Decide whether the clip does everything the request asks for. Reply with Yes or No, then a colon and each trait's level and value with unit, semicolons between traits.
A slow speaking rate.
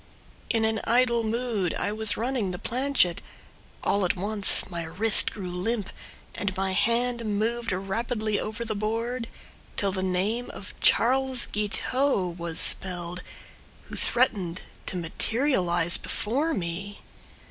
Yes: slow, 130 wpm